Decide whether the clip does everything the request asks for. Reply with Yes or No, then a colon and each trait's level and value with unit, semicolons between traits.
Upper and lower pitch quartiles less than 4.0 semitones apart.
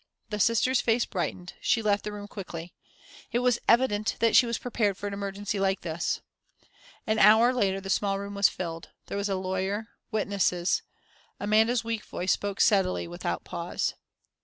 Yes: average, 2.7 semitones